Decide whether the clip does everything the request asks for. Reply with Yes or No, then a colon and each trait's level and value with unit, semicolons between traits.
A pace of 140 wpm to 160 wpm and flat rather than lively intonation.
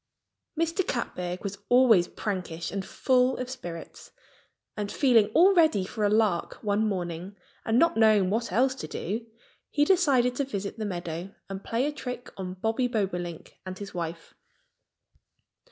No: average, 155 wpm; average, 5.3 semitones